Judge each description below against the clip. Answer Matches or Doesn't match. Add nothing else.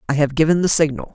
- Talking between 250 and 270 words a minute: Matches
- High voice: Doesn't match